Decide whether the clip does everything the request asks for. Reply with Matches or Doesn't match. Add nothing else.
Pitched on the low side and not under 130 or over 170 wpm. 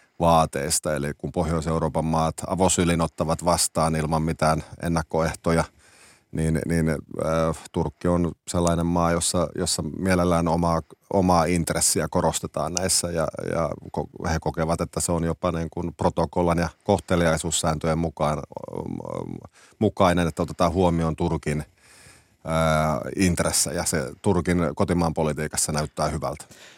Doesn't match